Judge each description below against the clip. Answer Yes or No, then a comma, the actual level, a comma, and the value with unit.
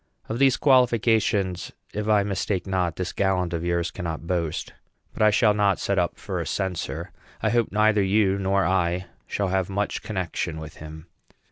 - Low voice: Yes, very low, 95 Hz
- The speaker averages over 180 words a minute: No, average, 175 wpm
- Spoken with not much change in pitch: No, average, 3.1 semitones